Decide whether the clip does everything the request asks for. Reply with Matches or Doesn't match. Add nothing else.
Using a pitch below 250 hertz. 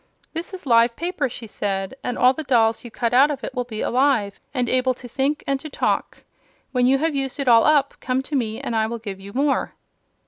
Doesn't match